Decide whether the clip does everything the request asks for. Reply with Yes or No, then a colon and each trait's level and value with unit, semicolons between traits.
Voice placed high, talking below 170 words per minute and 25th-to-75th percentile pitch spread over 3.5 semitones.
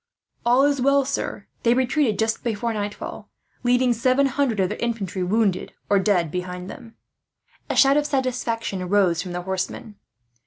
Yes: high, 225 Hz; average, 160 wpm; average, 5.2 semitones